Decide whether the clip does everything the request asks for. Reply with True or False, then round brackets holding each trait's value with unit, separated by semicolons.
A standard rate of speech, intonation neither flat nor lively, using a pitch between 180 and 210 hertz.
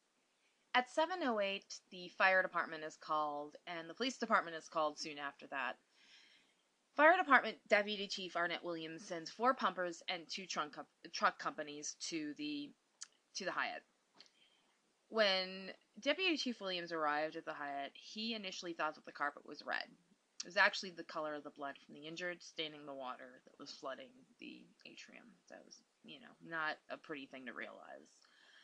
False (170 wpm; 7.7 semitones; 185 Hz)